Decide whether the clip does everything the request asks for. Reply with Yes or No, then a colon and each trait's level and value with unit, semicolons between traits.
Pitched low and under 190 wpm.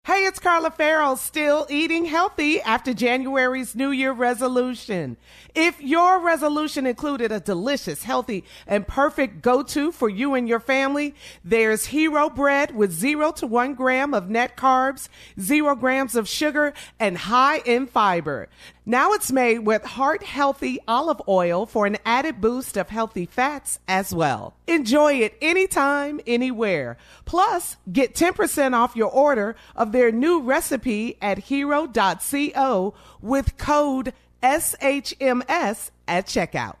No: very high, 265 Hz; average, 140 wpm